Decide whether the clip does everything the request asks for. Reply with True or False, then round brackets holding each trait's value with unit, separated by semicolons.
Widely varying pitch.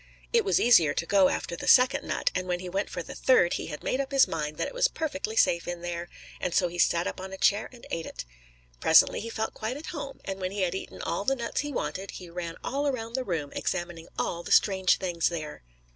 True (6.6 semitones)